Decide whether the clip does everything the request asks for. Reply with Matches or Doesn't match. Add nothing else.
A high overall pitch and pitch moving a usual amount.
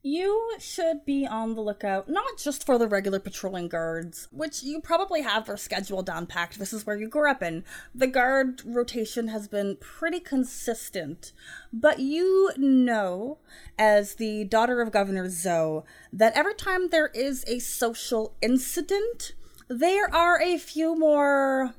Doesn't match